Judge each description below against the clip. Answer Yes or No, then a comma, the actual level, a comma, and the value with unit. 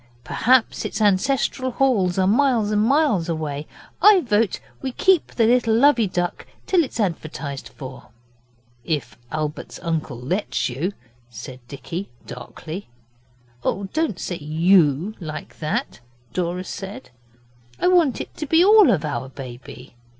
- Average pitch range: No, wide, 8.5 semitones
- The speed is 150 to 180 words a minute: No, slow, 135 wpm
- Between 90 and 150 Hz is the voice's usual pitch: No, medium, 185 Hz